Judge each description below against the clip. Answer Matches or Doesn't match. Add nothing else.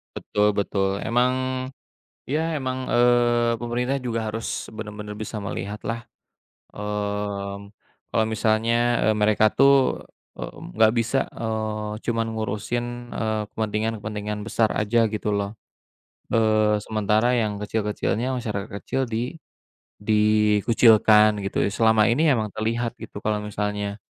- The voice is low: Matches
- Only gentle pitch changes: Matches